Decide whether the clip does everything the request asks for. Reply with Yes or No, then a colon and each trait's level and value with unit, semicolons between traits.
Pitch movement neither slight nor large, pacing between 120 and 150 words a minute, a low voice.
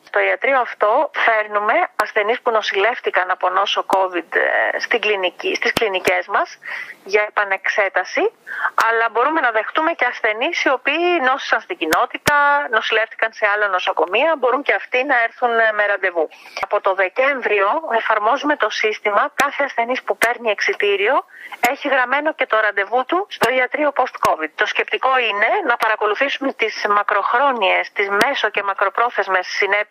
No: average, 4.7 semitones; average, 140 wpm; high, 225 Hz